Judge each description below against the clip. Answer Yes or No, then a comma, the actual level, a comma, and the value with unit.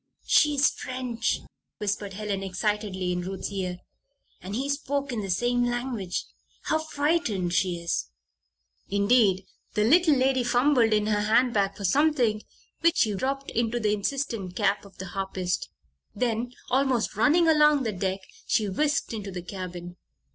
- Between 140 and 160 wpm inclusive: Yes, average, 150 wpm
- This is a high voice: Yes, high, 215 Hz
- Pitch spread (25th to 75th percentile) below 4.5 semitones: No, average, 5.2 semitones